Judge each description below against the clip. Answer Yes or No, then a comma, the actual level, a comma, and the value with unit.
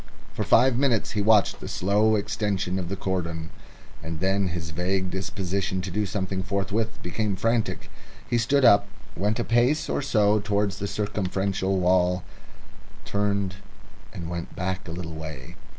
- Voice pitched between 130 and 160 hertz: No, low, 100 Hz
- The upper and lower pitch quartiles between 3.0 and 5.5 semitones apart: No, narrow, 2.6 semitones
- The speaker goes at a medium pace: Yes, average, 155 wpm